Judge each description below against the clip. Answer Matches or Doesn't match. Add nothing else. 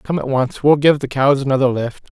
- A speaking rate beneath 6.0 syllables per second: Matches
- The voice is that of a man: Matches